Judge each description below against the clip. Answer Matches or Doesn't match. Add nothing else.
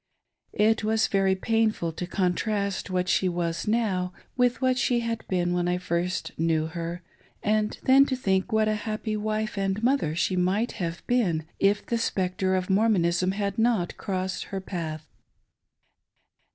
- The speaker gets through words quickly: Doesn't match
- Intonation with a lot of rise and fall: Doesn't match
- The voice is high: Matches